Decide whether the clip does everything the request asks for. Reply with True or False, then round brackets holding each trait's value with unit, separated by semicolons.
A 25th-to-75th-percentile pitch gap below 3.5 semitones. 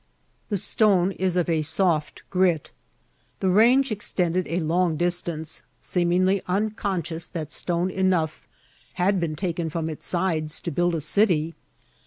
True (2.6 semitones)